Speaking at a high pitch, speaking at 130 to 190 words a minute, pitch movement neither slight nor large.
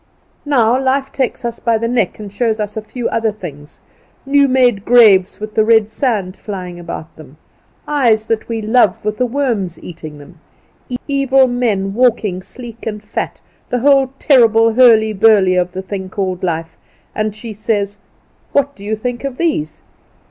Yes: high, 220 Hz; average, 170 wpm; average, 4.1 semitones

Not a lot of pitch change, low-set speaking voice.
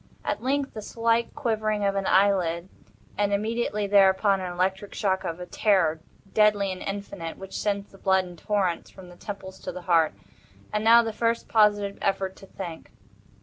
No: narrow, 2.1 semitones; high, 200 Hz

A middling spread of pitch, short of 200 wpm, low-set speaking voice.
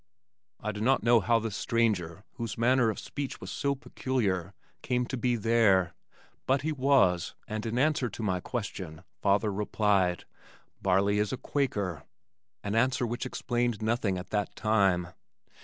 Yes: average, 3.9 semitones; average, 155 wpm; low, 110 Hz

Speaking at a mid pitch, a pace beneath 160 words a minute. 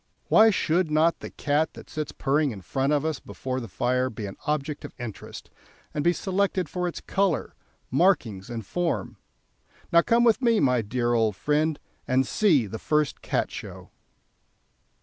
No: medium, 150 Hz; average, 170 wpm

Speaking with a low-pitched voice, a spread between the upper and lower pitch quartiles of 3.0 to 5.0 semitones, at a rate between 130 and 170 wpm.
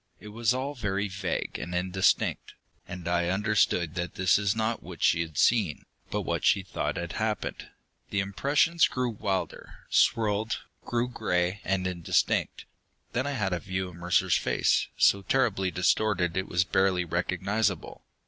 Yes: very low, 95 Hz; average, 3.4 semitones; average, 160 wpm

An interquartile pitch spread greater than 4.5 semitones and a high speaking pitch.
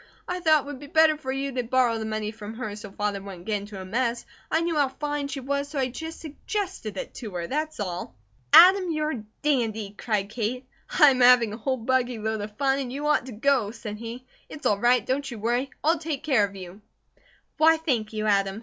Yes: average, 5.2 semitones; very high, 250 Hz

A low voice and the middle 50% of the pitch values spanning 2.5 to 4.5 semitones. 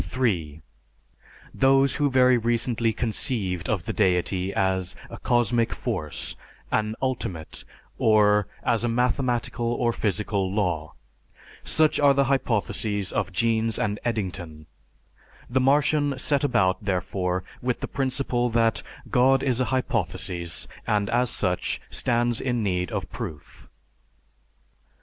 No: low, 115 Hz; average, 4.9 semitones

